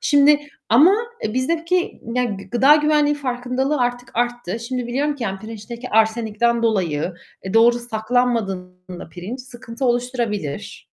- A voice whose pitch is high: Yes, high, 240 Hz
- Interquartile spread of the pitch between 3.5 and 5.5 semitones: No, average, 3.0 semitones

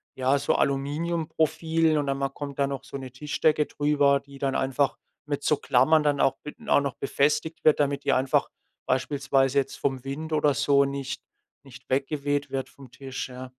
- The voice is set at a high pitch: No, medium, 140 Hz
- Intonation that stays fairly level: Yes, narrow, 1.6 semitones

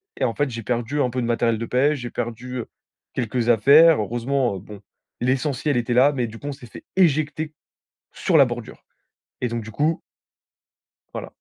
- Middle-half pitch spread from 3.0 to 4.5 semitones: Yes, average, 3.5 semitones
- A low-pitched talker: Yes, low, 125 Hz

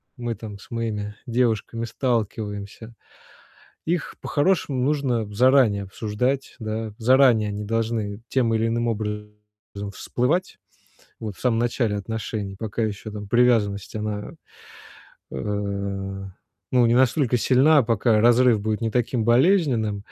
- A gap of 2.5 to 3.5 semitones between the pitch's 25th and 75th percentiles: Yes, average, 3.0 semitones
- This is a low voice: Yes, low, 115 Hz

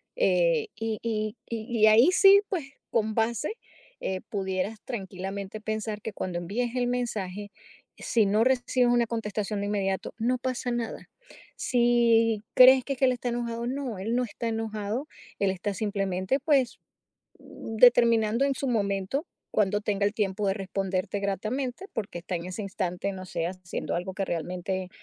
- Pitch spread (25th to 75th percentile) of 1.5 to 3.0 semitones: No, average, 3.7 semitones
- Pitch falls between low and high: No, high, 215 Hz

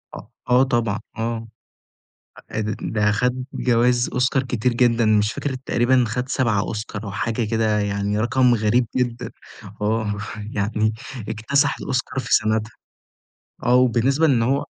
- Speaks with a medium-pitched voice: No, low, 115 Hz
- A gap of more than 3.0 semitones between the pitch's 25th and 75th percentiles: No, average, 2.7 semitones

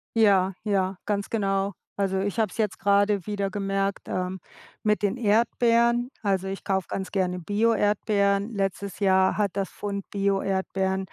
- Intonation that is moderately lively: No, narrow, 1.5 semitones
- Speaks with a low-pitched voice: No, high, 200 Hz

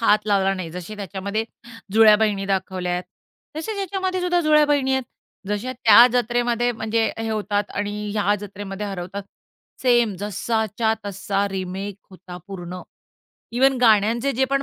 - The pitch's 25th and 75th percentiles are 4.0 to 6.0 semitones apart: No, average, 3.6 semitones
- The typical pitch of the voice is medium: No, high, 210 Hz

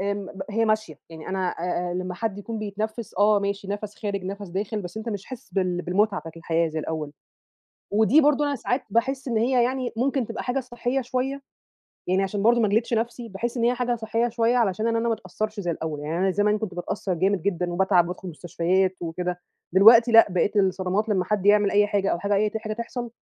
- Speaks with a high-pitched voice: Yes, high, 205 Hz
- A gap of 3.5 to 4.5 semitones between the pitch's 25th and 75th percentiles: Yes, average, 3.8 semitones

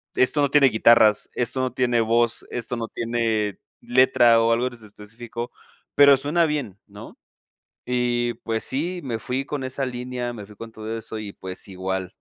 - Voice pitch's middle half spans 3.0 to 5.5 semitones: No, narrow, 2.6 semitones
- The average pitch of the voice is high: No, low, 120 Hz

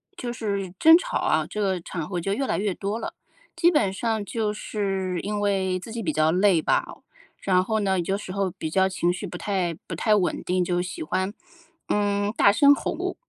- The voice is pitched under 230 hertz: Yes, high, 195 Hz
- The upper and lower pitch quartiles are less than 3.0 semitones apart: Yes, narrow, 2.5 semitones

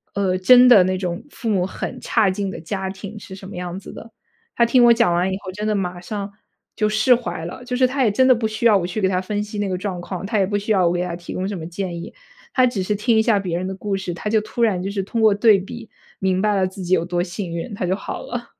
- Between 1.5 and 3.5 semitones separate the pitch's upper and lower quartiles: Yes, average, 2.9 semitones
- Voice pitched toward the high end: Yes, high, 195 Hz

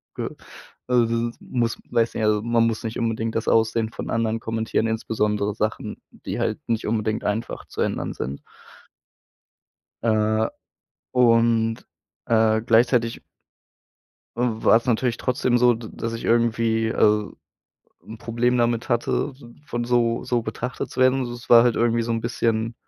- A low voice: Yes, low, 115 Hz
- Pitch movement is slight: Yes, narrow, 1.1 semitones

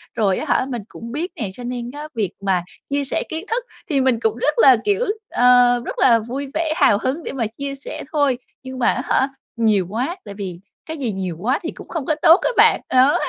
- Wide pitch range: No, average, 4.4 semitones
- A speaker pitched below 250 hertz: No, very high, 255 Hz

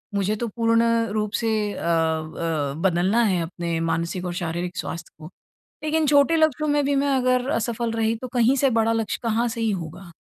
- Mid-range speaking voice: No, high, 220 Hz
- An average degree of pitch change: No, wide, 6.1 semitones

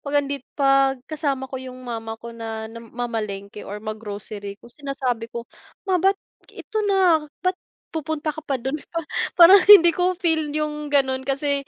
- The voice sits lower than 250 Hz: No, very high, 275 Hz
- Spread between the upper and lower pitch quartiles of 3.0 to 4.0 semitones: No, average, 5.3 semitones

